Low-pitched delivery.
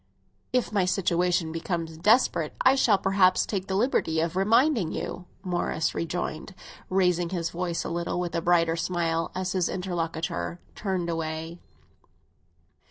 No: medium, 175 Hz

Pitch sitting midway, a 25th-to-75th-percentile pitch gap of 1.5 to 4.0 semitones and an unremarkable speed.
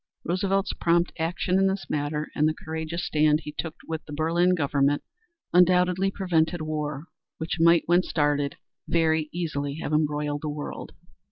Yes: medium, 160 Hz; average, 2.7 semitones; average, 155 wpm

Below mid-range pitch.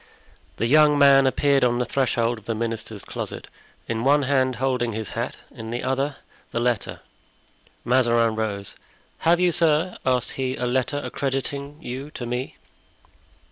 Yes: low, 130 Hz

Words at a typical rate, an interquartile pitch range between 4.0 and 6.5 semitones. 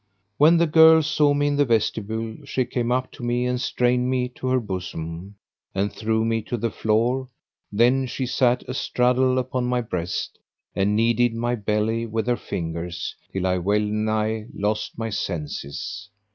No: average, 170 wpm; average, 3.2 semitones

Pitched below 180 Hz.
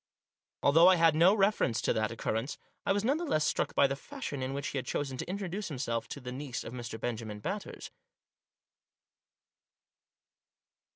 Yes: medium, 140 Hz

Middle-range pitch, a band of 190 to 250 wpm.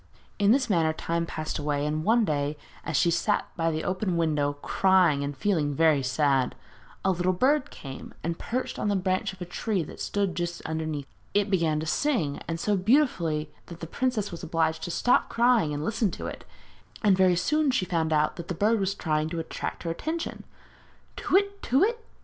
Yes: medium, 175 Hz; average, 200 wpm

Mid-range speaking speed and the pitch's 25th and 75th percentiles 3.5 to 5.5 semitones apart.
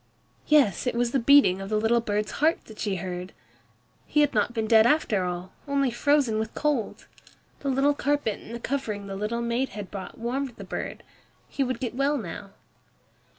Yes: average, 195 wpm; average, 4.9 semitones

